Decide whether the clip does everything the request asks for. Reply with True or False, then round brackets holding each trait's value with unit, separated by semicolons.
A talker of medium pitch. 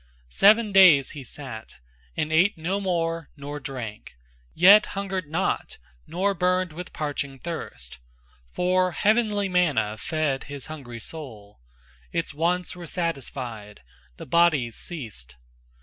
True (160 Hz)